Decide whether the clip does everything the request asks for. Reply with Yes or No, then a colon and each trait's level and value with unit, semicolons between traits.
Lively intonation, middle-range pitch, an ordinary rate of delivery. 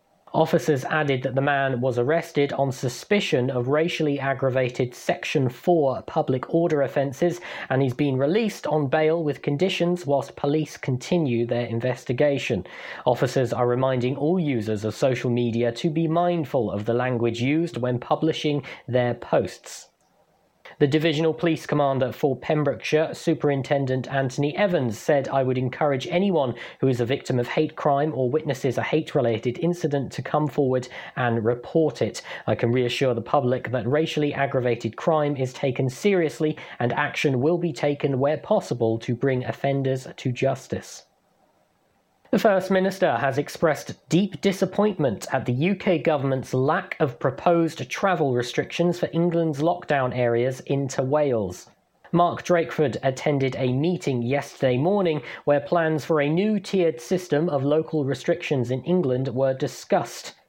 No: average, 3.8 semitones; medium, 145 Hz; average, 150 wpm